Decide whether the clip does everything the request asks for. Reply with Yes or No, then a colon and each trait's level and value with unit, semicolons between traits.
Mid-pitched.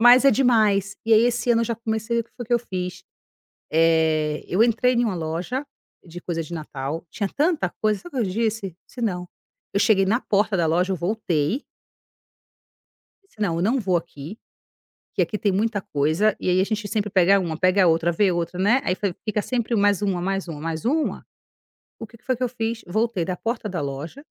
No: high, 200 Hz